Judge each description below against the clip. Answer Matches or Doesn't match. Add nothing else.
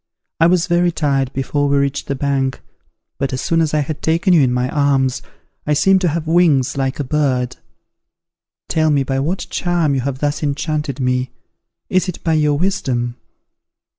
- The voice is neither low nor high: Matches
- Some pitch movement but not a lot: Matches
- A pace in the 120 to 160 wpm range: Doesn't match